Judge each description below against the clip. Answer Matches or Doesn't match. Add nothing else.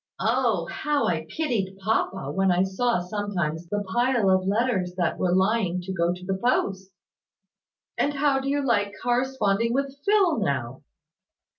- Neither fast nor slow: Matches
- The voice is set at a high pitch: Matches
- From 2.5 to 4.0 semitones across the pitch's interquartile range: Doesn't match